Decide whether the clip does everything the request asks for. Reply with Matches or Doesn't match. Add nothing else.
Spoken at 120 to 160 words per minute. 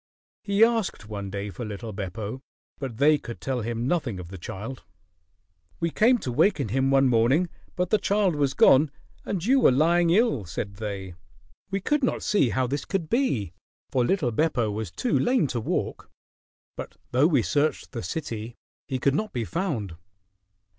Doesn't match